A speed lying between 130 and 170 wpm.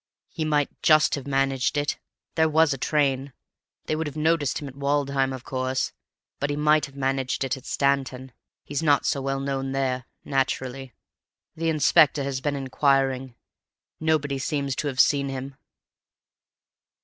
Yes: average, 160 wpm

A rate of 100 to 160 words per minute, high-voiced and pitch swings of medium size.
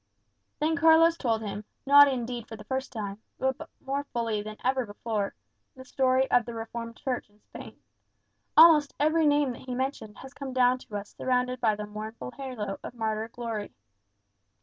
No: average, 175 wpm; high, 245 Hz; average, 3.6 semitones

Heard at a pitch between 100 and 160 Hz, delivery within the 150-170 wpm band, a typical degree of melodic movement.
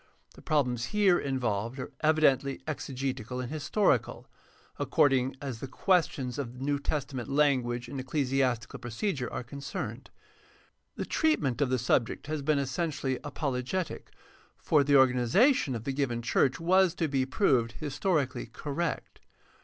No: low, 135 Hz; average, 140 wpm; average, 3.4 semitones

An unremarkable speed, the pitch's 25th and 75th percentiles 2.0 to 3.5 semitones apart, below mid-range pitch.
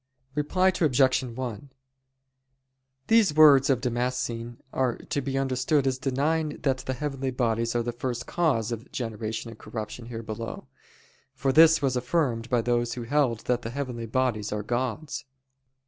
Yes: average, 155 wpm; average, 3.1 semitones; low, 125 Hz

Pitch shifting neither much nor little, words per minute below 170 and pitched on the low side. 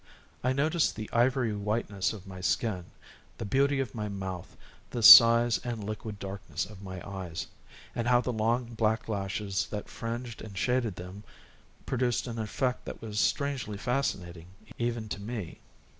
Yes: average, 3.4 semitones; average, 160 wpm; low, 110 Hz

